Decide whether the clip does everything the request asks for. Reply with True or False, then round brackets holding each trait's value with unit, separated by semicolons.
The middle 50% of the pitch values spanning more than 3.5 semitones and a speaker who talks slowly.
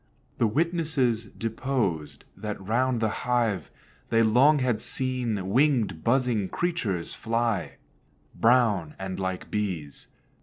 True (4.5 semitones; 110 wpm)